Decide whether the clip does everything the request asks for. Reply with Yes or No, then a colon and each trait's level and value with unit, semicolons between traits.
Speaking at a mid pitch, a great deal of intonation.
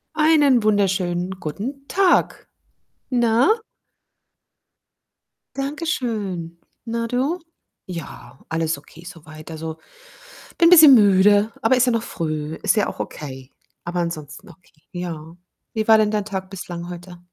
No: high, 195 Hz; wide, 6.1 semitones